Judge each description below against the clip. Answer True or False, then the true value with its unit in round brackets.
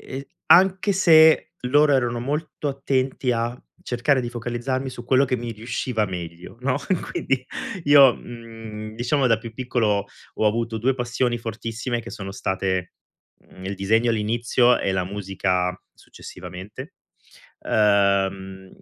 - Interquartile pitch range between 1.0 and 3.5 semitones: False (4.2 semitones)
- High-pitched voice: False (120 Hz)